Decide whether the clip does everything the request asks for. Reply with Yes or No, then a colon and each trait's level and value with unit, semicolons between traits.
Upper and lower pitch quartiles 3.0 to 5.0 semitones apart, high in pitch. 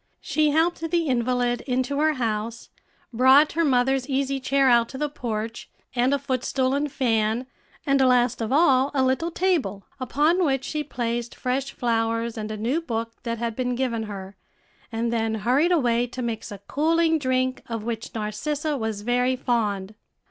Yes: average, 3.4 semitones; very high, 250 Hz